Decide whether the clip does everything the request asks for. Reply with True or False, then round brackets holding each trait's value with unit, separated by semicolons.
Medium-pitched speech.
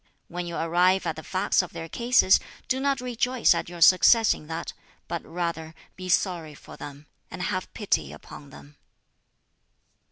True (175 Hz)